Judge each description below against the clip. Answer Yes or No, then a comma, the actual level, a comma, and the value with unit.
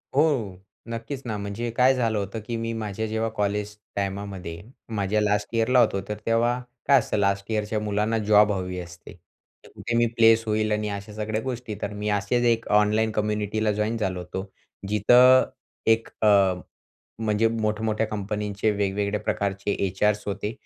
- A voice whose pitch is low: Yes, low, 105 Hz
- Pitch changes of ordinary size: No, narrow, 1.9 semitones